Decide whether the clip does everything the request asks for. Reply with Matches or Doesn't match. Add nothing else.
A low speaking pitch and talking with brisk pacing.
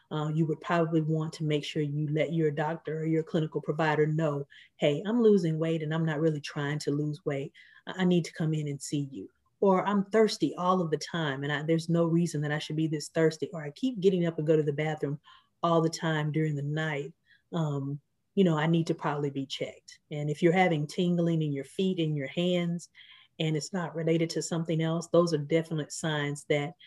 Doesn't match